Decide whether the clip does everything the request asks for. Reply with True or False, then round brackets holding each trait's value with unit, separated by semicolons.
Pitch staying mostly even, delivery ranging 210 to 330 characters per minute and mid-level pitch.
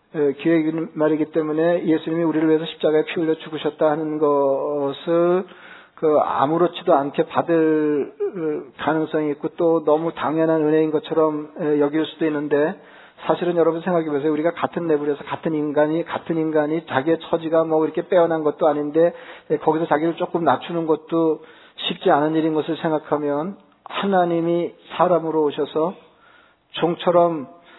False (1.7 semitones; 340 characters per minute; 160 Hz)